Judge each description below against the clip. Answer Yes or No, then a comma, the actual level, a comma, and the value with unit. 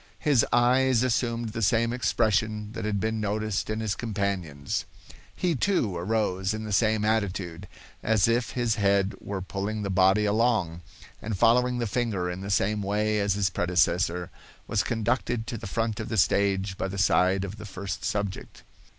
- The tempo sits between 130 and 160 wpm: No, average, 175 wpm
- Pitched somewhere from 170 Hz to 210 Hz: No, low, 105 Hz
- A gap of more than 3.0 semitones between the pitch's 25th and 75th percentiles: No, average, 2.7 semitones